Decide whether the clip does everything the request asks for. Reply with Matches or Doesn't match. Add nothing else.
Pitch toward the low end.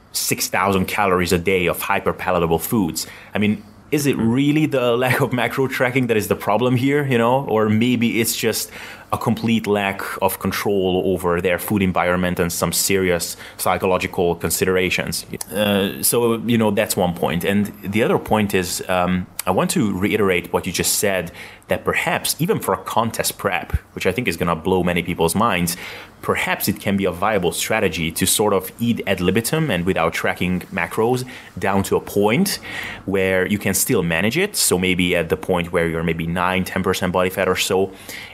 Matches